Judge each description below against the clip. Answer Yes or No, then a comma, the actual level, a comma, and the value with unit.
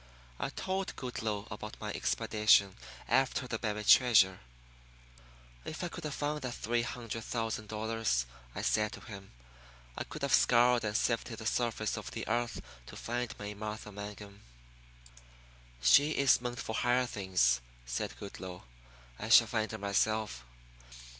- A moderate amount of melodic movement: Yes, average, 3.0 semitones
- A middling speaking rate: Yes, average, 150 wpm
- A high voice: No, low, 110 Hz